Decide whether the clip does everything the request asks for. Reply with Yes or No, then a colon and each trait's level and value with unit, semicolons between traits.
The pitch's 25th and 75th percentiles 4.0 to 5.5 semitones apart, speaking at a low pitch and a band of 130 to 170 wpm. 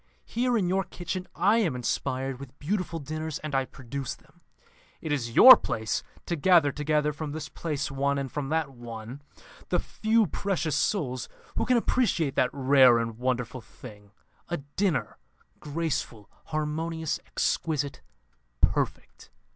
No: average, 4.3 semitones; medium, 150 Hz; average, 145 wpm